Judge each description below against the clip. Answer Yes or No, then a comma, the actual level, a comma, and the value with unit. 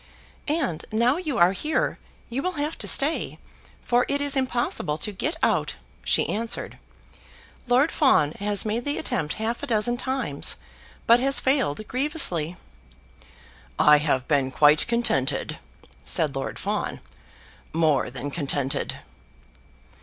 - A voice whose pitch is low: No, high, 230 Hz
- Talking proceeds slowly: Yes, slow, 130 wpm